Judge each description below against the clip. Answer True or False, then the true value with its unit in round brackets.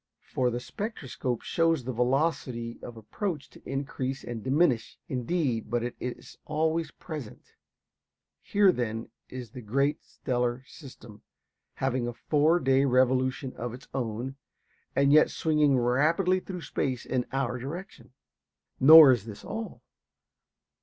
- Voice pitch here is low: True (130 Hz)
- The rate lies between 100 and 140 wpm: True (135 wpm)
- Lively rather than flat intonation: False (3.9 semitones)